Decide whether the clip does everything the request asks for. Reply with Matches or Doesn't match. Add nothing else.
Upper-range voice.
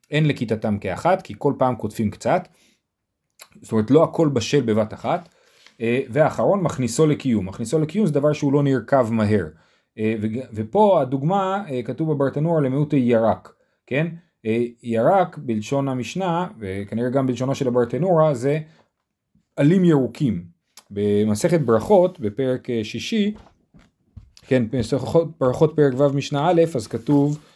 Doesn't match